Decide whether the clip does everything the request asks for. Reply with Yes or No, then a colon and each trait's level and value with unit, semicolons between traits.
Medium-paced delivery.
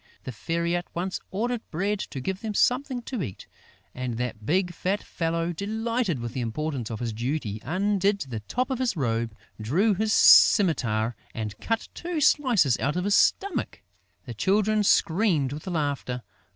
Yes: average, 165 wpm